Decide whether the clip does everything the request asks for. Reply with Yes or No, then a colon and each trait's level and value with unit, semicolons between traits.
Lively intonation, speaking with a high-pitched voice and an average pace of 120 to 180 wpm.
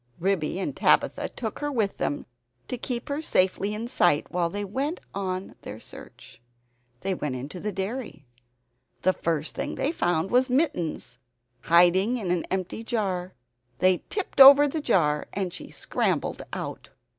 Yes: wide, 6.0 semitones; high, 195 Hz; average, 160 wpm